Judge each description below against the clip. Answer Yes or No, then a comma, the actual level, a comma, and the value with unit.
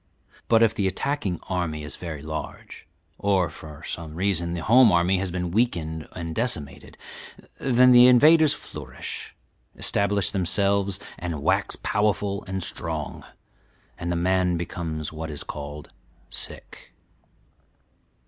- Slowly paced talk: Yes, slow, 130 wpm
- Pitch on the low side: Yes, very low, 90 Hz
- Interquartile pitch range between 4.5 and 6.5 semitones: No, average, 4.1 semitones